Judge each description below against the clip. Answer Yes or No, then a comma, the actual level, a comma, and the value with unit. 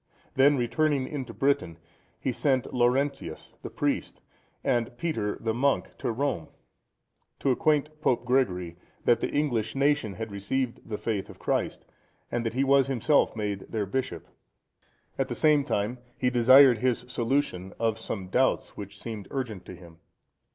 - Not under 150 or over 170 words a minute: Yes, average, 160 wpm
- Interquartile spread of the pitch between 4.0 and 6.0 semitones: Yes, average, 4.3 semitones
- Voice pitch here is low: Yes, low, 120 Hz